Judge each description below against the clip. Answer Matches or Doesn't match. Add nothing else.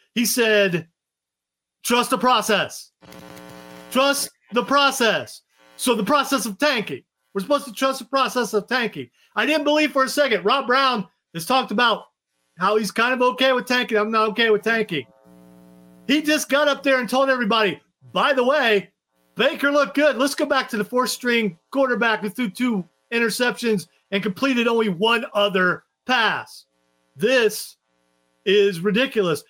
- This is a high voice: Matches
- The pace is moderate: Matches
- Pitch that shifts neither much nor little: Doesn't match